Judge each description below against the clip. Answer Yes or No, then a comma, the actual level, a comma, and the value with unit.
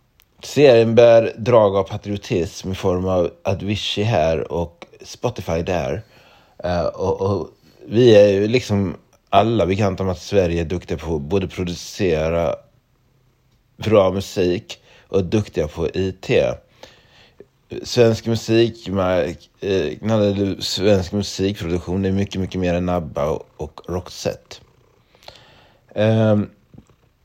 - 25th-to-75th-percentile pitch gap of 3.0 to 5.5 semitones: Yes, average, 3.7 semitones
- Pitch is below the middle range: Yes, low, 100 Hz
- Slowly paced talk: Yes, slow, 120 wpm